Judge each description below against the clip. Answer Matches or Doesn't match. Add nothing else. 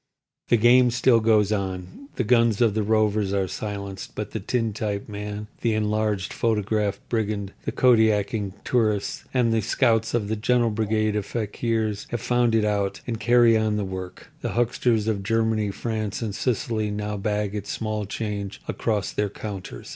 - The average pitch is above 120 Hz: Doesn't match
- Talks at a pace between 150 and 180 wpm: Matches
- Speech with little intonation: Matches